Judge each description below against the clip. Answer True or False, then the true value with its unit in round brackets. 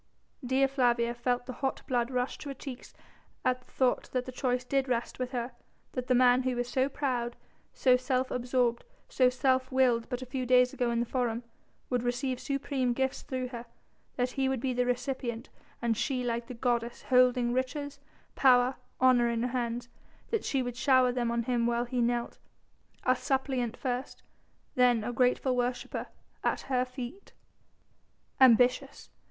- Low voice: False (250 Hz)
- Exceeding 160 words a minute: True (175 wpm)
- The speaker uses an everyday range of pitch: False (1.3 semitones)